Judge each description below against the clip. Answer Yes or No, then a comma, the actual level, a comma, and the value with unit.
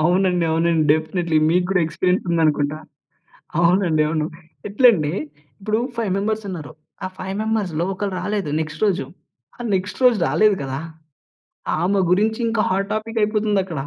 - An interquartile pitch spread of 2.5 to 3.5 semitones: No, average, 4.3 semitones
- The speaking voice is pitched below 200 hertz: Yes, medium, 185 Hz